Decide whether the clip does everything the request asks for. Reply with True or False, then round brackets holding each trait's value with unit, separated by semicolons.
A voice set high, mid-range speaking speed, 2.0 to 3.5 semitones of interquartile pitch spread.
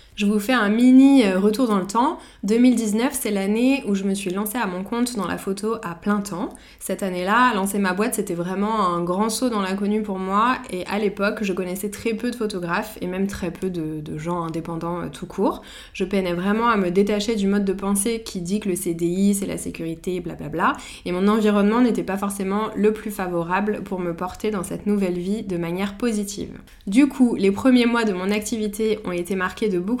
False (205 Hz; 225 wpm; 2.8 semitones)